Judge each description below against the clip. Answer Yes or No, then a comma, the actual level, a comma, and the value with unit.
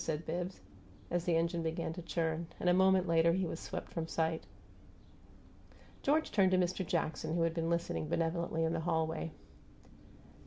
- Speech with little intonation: Yes, narrow, 1.6 semitones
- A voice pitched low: No, medium, 170 Hz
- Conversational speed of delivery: Yes, average, 170 wpm